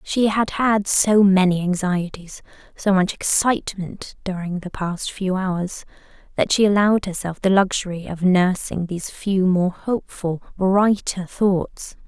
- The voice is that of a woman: Yes, female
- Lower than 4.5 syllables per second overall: Yes, 4.2 syllables/s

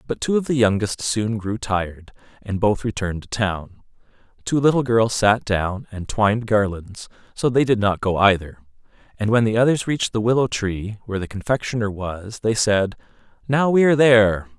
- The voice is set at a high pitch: No, low, 110 Hz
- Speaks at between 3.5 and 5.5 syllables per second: Yes, 5.2 syllables/s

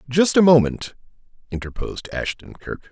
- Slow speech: Yes, slow, 125 wpm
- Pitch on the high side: No, medium, 140 Hz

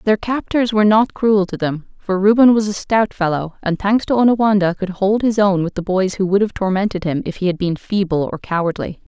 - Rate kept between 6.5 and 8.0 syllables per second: No, 5.5 syllables/s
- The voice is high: Yes, high, 195 Hz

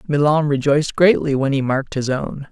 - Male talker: Yes, male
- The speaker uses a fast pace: No, average, 190 wpm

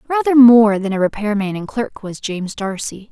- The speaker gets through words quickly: Yes, fast, 210 wpm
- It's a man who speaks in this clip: No, female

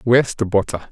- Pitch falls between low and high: No, low, 110 Hz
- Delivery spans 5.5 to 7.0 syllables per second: Yes, 6.2 syllables/s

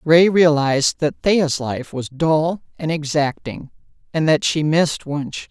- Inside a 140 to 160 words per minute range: Yes, average, 155 wpm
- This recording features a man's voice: No, female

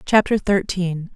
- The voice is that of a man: No, female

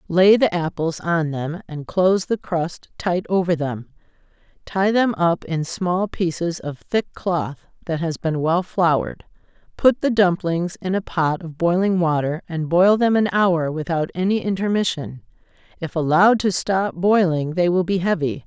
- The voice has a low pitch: No, medium, 175 Hz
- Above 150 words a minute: Yes, average, 160 wpm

